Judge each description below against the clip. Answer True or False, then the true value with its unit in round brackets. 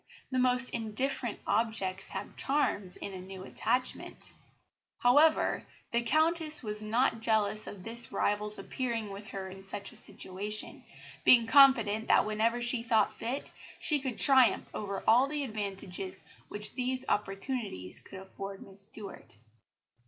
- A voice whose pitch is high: True (220 Hz)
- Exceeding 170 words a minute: False (140 wpm)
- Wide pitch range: False (4.1 semitones)